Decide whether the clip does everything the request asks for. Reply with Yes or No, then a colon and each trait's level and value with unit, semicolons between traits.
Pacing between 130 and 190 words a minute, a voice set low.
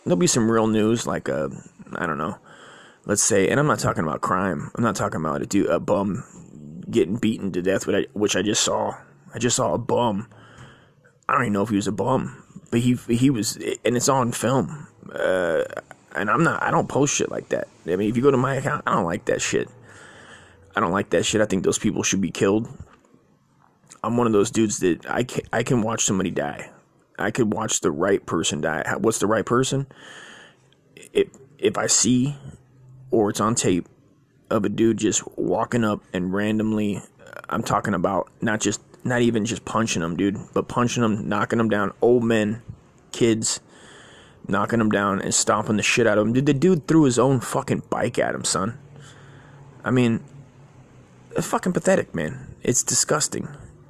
No: average, 200 wpm; low, 115 Hz